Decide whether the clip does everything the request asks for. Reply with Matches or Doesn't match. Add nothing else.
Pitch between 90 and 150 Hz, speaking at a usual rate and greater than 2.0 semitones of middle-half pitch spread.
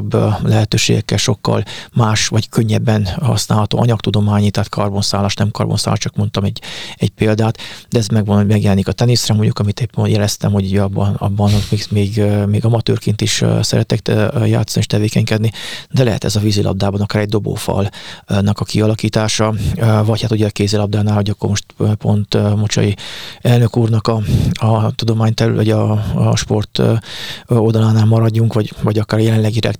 Doesn't match